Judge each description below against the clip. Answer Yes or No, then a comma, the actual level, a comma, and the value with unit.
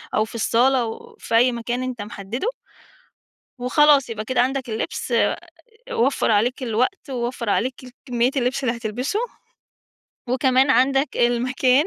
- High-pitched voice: Yes, very high, 250 Hz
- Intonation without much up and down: Yes, narrow, 2.2 semitones